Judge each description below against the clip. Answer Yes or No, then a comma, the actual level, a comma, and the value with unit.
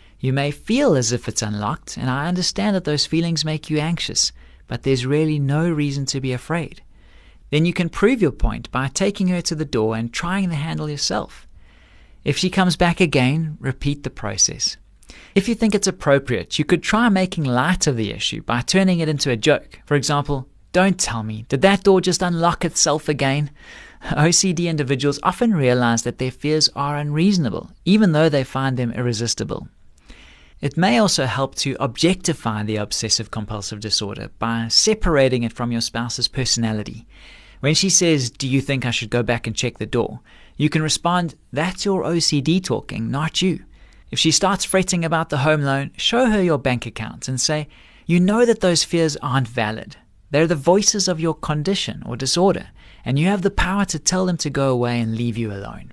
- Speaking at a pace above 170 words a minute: Yes, average, 195 wpm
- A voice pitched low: No, medium, 145 Hz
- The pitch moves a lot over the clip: Yes, wide, 6.2 semitones